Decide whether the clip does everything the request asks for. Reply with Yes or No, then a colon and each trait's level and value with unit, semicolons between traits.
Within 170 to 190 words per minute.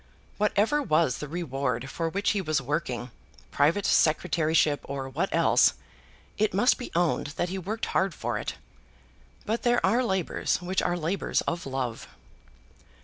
No: average, 150 wpm